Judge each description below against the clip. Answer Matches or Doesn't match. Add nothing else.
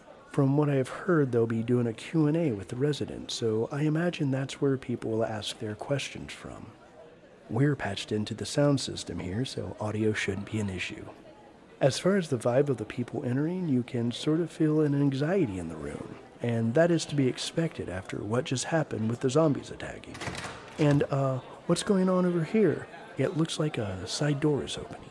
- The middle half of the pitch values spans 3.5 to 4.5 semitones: Doesn't match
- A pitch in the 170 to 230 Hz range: Doesn't match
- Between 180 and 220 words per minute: Matches